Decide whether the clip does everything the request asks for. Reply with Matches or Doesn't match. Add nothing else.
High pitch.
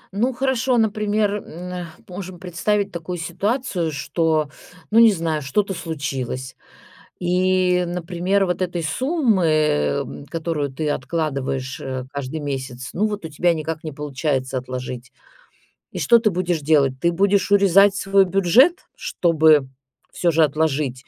Doesn't match